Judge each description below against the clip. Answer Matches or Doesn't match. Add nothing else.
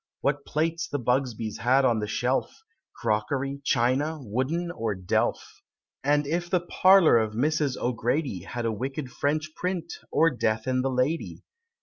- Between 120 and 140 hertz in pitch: Matches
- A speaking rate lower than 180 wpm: Matches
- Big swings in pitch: Doesn't match